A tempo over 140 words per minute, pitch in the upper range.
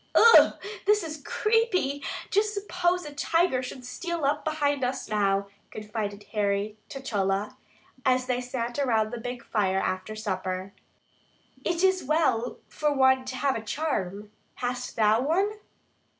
No: slow, 135 wpm; very high, 255 Hz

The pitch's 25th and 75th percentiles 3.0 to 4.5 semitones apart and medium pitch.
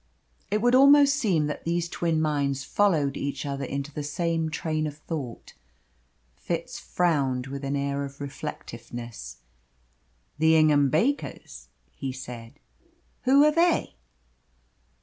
Yes: average, 3.8 semitones; medium, 150 Hz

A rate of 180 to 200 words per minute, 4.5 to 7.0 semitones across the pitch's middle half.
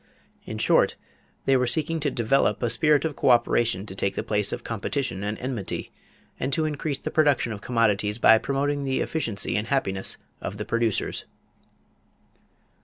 No: average, 165 wpm; average, 5.1 semitones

